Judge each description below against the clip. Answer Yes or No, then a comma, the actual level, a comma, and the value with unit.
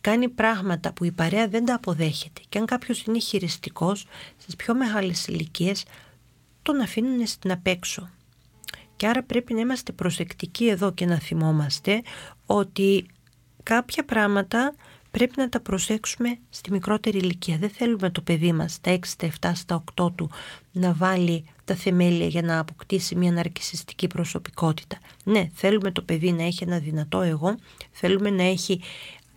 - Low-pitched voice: No, medium, 185 Hz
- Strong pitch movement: No, average, 4.1 semitones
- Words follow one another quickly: No, average, 155 wpm